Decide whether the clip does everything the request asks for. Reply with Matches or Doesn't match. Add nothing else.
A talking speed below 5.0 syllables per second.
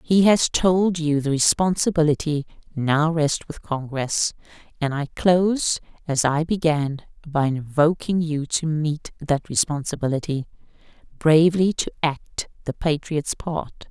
Matches